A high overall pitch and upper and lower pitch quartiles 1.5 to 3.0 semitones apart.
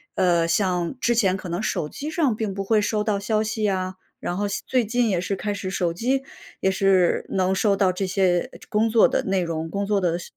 Yes: high, 195 Hz; average, 2.7 semitones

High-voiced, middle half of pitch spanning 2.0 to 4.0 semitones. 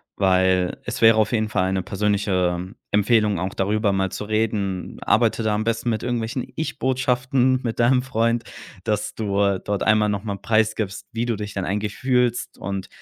No: low, 105 Hz; average, 2.9 semitones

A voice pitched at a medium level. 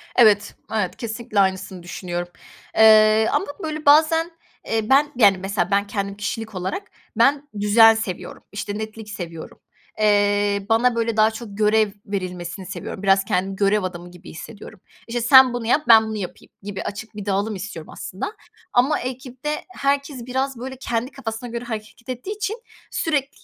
No: high, 220 Hz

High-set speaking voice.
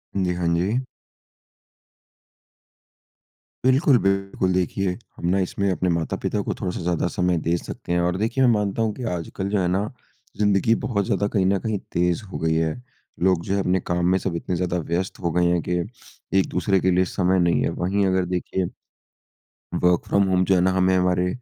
No: very low, 95 Hz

